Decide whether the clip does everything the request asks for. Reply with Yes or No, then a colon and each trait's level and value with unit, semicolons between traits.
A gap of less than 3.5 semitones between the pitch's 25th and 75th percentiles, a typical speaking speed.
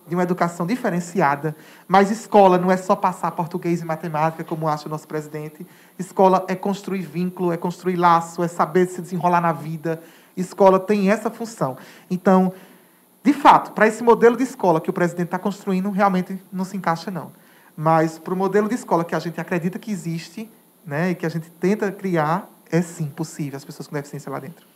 No: average, 2.7 semitones; fast, 195 wpm